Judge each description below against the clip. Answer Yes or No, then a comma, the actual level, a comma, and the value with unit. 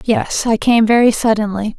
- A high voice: Yes, high, 220 Hz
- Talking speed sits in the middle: Yes, average, 170 wpm